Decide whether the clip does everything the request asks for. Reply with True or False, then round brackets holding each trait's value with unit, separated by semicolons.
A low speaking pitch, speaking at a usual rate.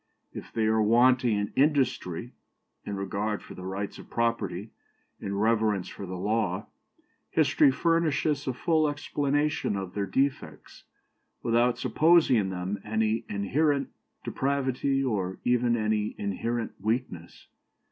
False (115 Hz; 125 wpm)